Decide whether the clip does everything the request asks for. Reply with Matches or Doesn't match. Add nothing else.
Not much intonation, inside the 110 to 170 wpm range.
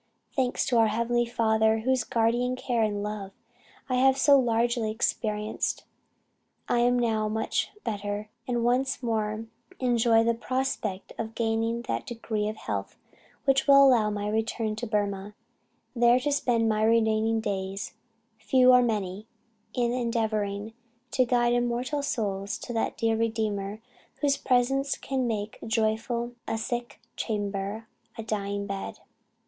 Matches